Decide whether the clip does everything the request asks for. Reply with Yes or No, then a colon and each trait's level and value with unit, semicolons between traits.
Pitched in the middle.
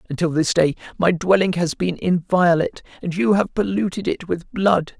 Yes: medium, 175 Hz